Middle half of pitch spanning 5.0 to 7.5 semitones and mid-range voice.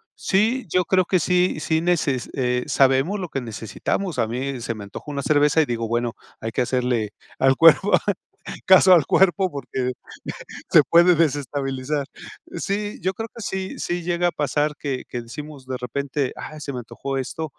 Yes: wide, 5.6 semitones; medium, 145 Hz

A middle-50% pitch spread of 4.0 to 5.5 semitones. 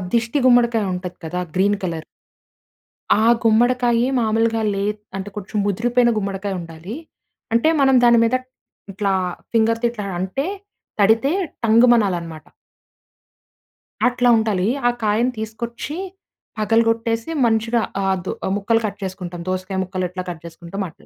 No: average, 3.5 semitones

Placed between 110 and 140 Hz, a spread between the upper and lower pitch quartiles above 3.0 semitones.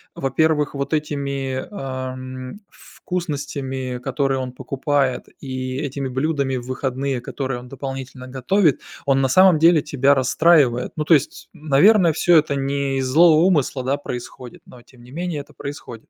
No: low, 135 Hz; narrow, 2.5 semitones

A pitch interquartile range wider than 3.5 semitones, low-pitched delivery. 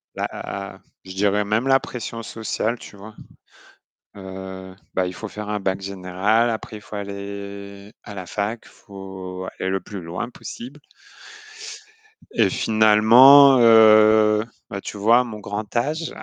No: narrow, 2.4 semitones; low, 105 Hz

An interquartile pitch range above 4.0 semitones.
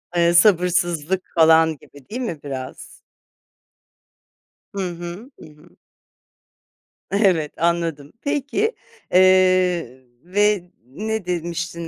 No: average, 2.8 semitones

